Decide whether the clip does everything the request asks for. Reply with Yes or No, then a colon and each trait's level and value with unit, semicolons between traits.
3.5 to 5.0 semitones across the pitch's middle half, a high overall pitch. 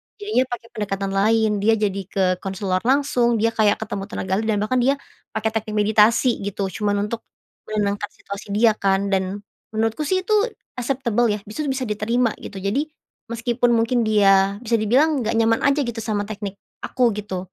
No: average, 2.8 semitones; high, 220 Hz